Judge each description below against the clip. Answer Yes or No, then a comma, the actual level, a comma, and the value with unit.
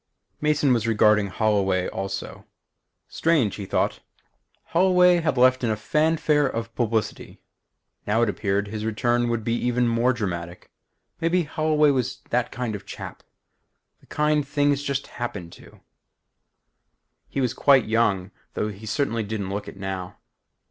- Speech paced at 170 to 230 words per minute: No, average, 150 wpm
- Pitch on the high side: No, low, 115 Hz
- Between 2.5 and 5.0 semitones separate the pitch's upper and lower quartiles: No, wide, 5.5 semitones